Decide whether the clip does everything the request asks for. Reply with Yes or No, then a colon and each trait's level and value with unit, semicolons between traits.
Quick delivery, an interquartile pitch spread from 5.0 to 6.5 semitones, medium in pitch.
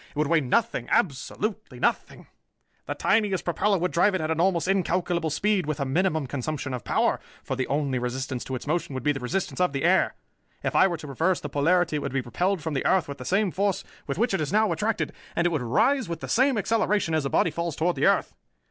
Yes: fast, 240 wpm; wide, 5.4 semitones; medium, 165 Hz